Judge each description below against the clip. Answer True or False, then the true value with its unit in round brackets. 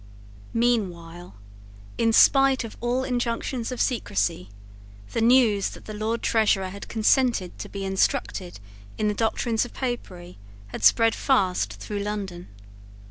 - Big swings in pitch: False (4.3 semitones)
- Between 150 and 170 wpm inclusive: False (135 wpm)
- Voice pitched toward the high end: True (220 Hz)